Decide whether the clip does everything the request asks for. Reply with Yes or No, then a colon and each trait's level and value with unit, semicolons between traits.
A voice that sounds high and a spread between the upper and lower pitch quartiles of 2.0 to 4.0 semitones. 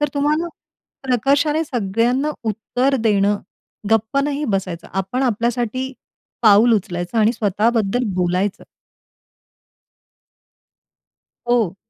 No: high, 230 Hz; average, 4.7 semitones